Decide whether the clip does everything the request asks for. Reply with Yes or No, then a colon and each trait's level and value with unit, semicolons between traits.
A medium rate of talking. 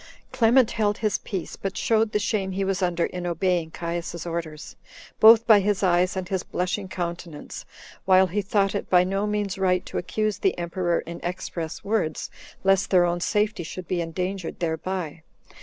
Yes: average, 175 wpm